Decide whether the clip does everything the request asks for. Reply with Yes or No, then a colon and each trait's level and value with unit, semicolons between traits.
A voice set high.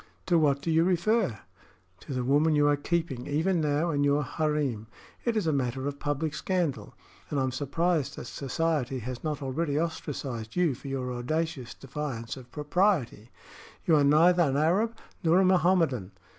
No: medium, 150 Hz